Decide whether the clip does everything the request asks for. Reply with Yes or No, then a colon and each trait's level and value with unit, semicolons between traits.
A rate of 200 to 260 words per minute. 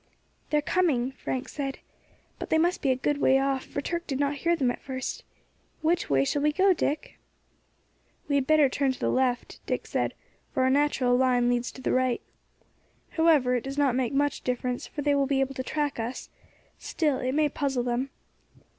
Yes: fast, 205 wpm